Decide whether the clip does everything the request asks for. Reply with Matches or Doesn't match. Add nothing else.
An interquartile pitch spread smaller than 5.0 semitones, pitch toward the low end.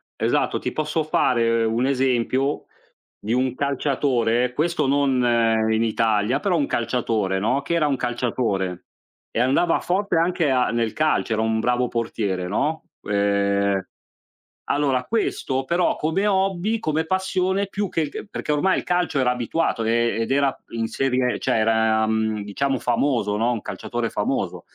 Doesn't match